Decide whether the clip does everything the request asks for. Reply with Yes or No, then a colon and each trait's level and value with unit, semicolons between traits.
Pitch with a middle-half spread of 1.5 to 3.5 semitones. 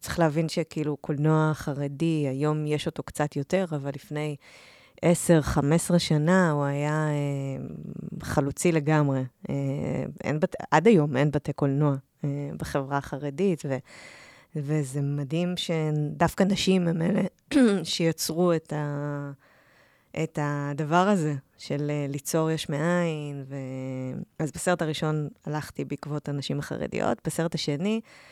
Yes: average, 2.7 semitones